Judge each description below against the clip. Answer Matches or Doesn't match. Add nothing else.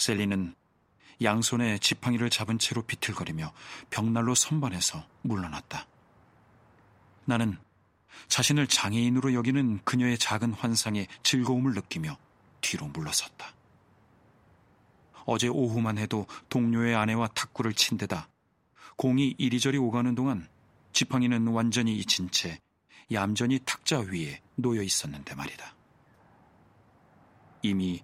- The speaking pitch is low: Matches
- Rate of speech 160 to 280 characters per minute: Matches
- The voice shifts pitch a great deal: Doesn't match